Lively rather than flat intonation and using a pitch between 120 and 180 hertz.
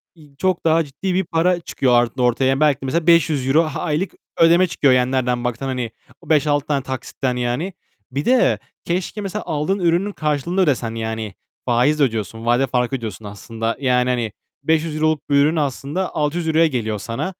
No: average, 4.9 semitones; medium, 140 Hz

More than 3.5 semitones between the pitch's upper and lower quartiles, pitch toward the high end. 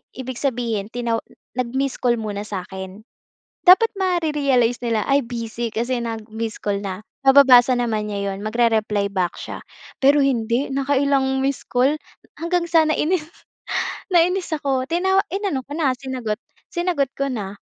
Yes: average, 4.3 semitones; very high, 255 Hz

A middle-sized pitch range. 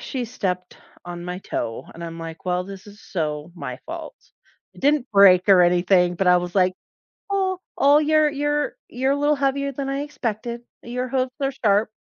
No: wide, 7.6 semitones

